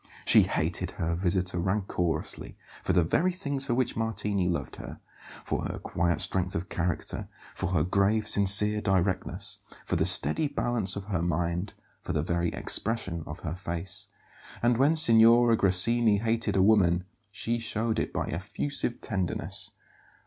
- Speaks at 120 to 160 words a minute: Yes, average, 155 wpm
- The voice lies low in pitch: Yes, very low, 95 Hz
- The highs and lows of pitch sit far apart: No, average, 4.4 semitones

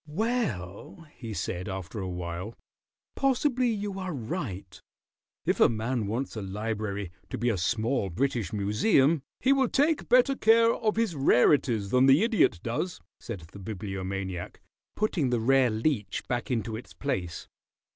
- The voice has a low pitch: Yes, low, 115 Hz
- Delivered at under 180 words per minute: Yes, average, 150 wpm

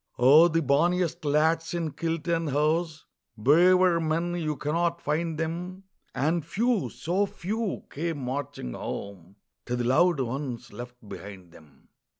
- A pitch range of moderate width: Yes, average, 4.3 semitones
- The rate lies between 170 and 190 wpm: No, average, 140 wpm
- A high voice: No, medium, 160 Hz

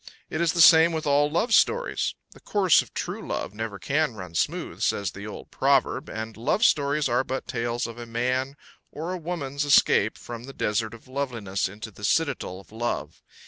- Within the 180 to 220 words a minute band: Yes, average, 195 wpm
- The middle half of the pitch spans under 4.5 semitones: No, wide, 5.4 semitones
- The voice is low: Yes, low, 130 Hz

